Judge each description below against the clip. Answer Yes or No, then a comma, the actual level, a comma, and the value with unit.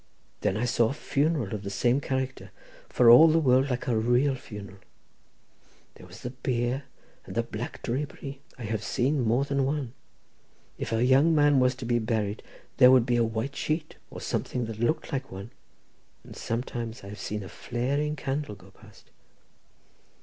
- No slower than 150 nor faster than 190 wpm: Yes, average, 180 wpm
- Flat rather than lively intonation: No, average, 3.5 semitones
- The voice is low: Yes, low, 125 Hz